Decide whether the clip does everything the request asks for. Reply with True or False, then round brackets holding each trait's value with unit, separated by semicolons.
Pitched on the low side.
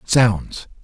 True (110 Hz)